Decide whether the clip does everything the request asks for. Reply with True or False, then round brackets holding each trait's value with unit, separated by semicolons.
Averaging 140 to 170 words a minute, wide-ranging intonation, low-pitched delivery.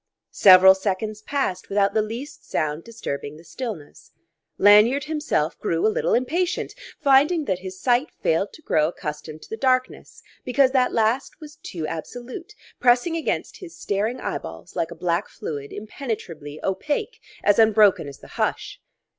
False (155 wpm; 7.4 semitones; 215 Hz)